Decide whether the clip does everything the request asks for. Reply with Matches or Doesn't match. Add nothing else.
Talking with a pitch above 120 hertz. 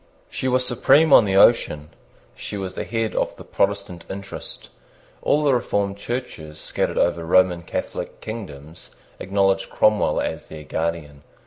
Doesn't match